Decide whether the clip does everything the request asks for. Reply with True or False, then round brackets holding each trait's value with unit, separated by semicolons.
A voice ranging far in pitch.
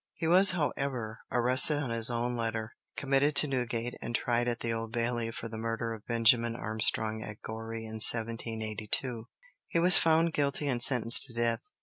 False (2.6 semitones)